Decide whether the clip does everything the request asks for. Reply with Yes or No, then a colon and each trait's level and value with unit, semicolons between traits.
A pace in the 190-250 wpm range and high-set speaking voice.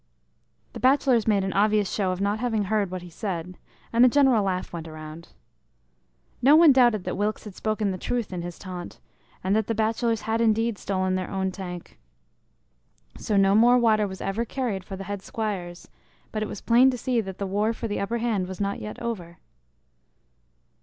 Yes: average, 195 wpm; high, 205 Hz